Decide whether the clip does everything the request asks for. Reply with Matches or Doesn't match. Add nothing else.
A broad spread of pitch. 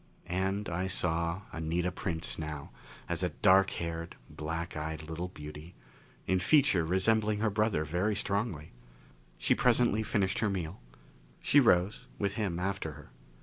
Doesn't match